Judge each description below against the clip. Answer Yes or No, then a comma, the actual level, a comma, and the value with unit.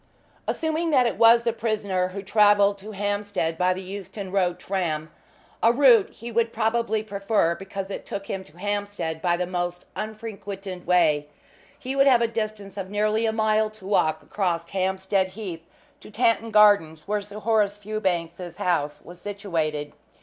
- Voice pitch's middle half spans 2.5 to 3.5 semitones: Yes, average, 3.1 semitones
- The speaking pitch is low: No, high, 200 Hz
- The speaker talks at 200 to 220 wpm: No, average, 165 wpm